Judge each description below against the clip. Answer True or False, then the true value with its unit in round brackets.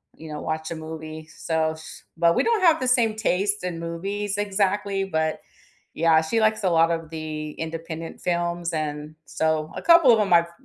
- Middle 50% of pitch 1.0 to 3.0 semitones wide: False (4.2 semitones)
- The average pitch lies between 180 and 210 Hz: False (170 Hz)